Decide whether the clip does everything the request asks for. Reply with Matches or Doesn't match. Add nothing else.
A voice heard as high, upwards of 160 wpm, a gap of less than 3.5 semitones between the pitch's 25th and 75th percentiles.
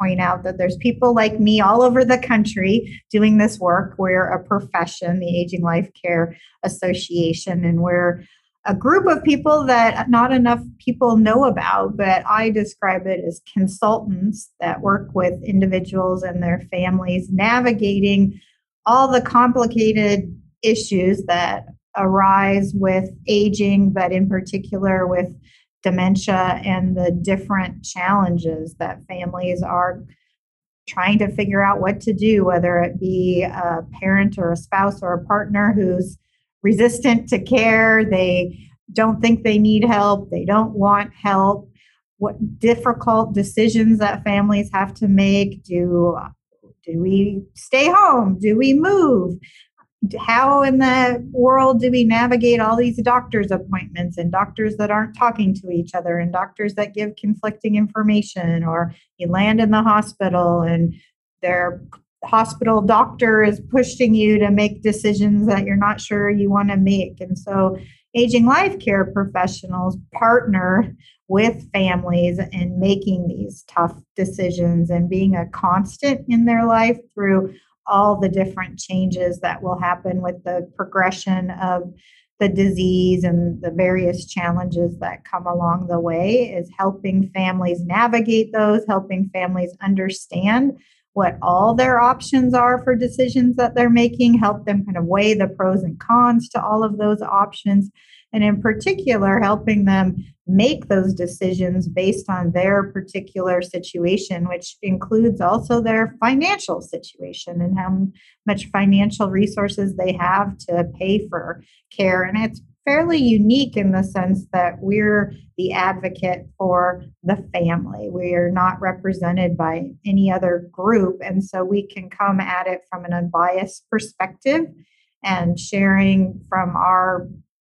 Doesn't match